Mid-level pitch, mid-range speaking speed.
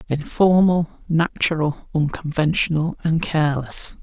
No: medium, 160 Hz; slow, 75 wpm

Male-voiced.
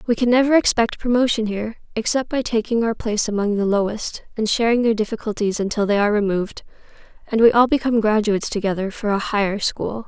No: female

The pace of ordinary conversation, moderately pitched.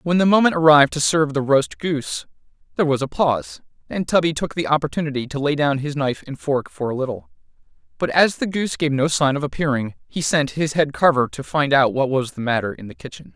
No: fast, 235 wpm; medium, 145 Hz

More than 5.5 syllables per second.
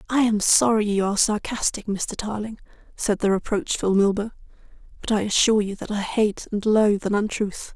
No: 5.4 syllables/s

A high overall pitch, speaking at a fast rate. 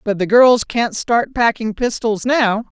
No: high, 225 Hz; average, 170 wpm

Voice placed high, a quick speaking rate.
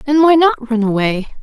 Yes: very high, 250 Hz; fast, 210 wpm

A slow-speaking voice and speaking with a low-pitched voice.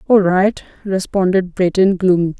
No: slow, 125 wpm; medium, 185 Hz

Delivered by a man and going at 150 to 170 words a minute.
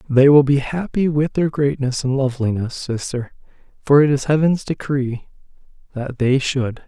Yes: male; average, 155 wpm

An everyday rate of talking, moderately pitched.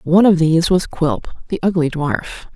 Yes: average, 190 wpm; medium, 170 Hz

